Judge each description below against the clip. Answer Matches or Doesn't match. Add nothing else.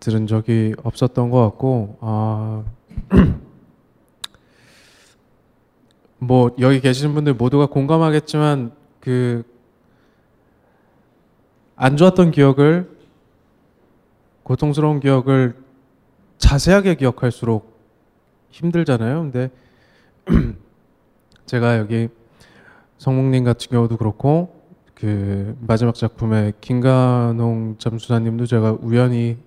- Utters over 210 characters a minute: Doesn't match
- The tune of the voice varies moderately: Matches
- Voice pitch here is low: Matches